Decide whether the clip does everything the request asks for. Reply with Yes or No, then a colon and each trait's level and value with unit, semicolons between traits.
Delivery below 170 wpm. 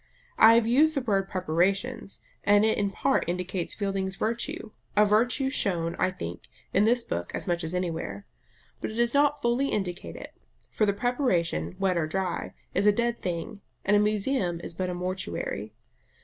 No: average, 180 wpm